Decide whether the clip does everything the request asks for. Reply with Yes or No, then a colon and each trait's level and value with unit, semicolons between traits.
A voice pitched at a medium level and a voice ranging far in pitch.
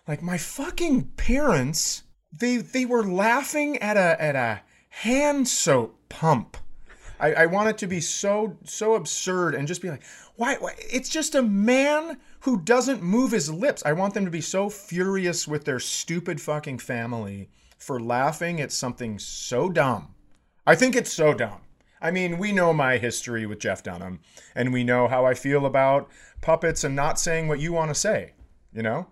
Yes: medium, 170 Hz; wide, 7.7 semitones